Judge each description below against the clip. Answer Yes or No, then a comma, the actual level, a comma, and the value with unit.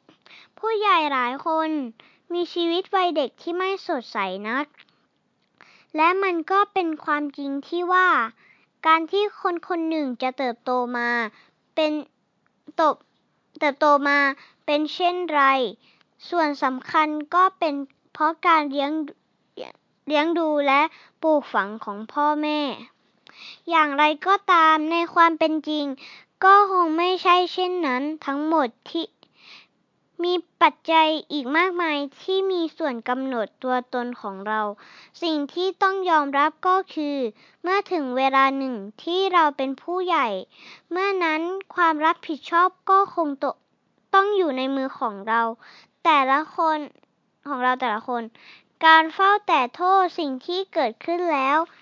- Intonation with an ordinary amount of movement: Yes, average, 4.4 semitones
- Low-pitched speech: No, very high, 310 Hz